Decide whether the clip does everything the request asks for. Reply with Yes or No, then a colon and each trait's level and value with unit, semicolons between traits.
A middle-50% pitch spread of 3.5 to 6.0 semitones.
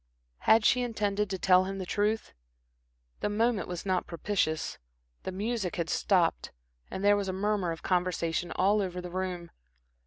No: narrow, 2.5 semitones